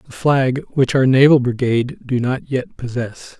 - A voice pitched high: No, low, 130 Hz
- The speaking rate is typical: Yes, average, 175 wpm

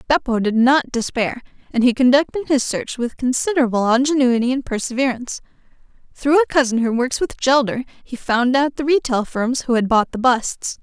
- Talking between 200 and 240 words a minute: No, average, 175 wpm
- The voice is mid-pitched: No, very high, 255 Hz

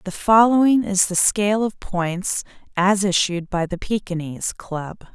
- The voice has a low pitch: No, high, 190 Hz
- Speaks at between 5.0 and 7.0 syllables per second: No, 4.3 syllables/s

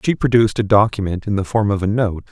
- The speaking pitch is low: Yes, low, 105 Hz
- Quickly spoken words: Yes, fast, 260 wpm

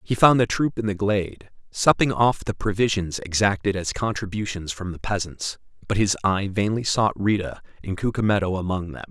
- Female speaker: No, male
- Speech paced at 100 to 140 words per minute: No, average, 180 wpm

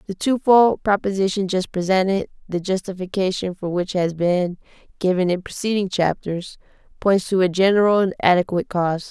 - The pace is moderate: Yes, average, 150 wpm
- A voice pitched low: No, high, 190 Hz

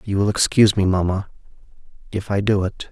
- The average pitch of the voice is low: Yes, low, 100 Hz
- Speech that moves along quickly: No, average, 185 wpm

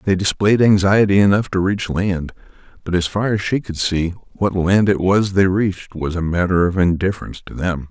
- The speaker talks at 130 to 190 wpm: No, fast, 205 wpm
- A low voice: Yes, very low, 95 Hz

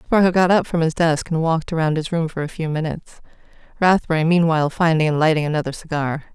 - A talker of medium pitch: Yes, medium, 160 Hz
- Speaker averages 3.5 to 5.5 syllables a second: No, 6.6 syllables/s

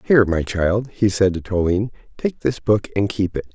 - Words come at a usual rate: No, fast, 220 wpm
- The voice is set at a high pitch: No, low, 100 Hz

